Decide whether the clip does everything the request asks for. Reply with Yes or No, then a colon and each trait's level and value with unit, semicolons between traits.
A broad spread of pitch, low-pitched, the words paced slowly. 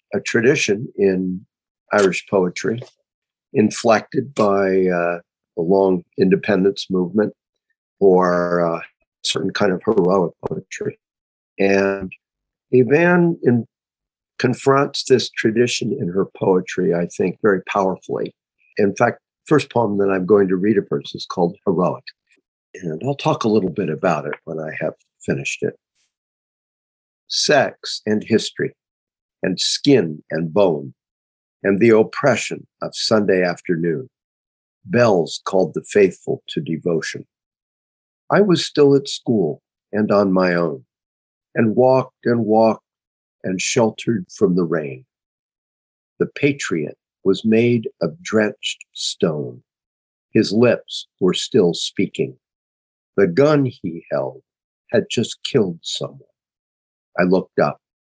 Yes: wide, 6.5 semitones; low, 100 Hz; slow, 125 wpm